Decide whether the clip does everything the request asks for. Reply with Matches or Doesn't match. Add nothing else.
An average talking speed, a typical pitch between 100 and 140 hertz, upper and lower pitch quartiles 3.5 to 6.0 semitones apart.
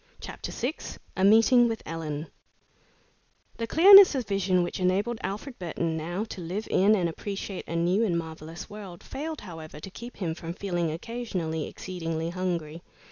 Doesn't match